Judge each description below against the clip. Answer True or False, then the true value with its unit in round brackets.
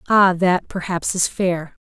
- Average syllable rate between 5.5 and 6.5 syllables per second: False (3.7 syllables/s)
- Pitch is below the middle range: False (180 Hz)